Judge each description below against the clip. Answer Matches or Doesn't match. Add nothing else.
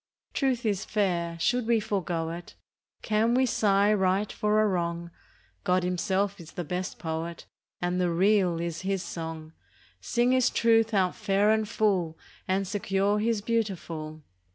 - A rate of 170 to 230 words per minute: Doesn't match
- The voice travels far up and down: Doesn't match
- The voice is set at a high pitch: Matches